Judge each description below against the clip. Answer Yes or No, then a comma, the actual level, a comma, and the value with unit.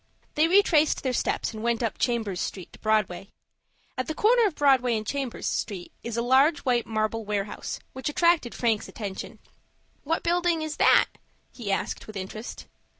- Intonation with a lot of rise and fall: Yes, wide, 5.9 semitones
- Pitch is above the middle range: Yes, high, 240 Hz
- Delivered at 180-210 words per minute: No, average, 170 wpm